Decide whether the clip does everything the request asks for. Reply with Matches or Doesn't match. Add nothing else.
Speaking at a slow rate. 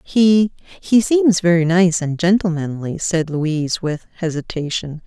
Matches